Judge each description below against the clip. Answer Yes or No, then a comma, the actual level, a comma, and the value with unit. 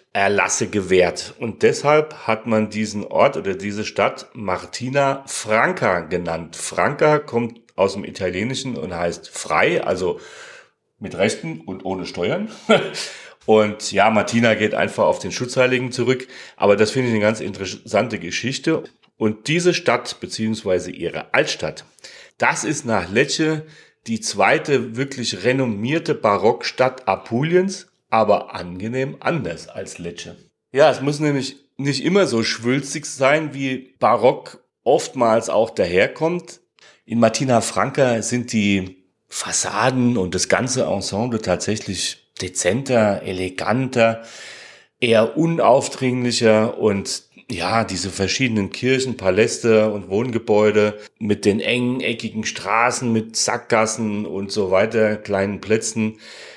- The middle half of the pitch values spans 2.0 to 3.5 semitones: No, average, 3.9 semitones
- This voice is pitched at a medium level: No, low, 115 Hz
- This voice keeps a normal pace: No, slow, 120 wpm